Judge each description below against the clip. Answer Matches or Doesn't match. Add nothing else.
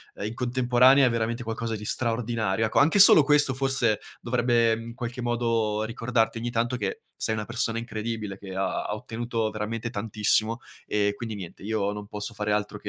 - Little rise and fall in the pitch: Matches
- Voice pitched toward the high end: Doesn't match